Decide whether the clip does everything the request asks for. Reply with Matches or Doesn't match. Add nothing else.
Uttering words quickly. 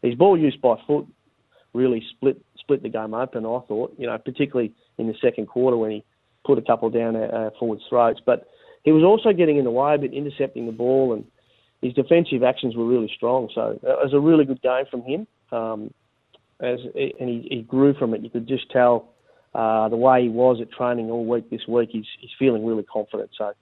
Matches